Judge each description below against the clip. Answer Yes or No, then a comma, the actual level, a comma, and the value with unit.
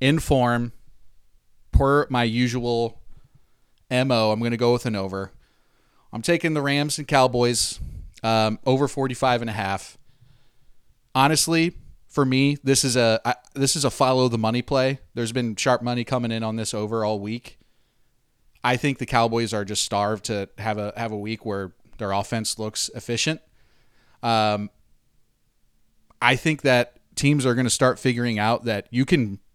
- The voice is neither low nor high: No, low, 120 Hz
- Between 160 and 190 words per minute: Yes, average, 165 wpm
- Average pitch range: Yes, average, 3.2 semitones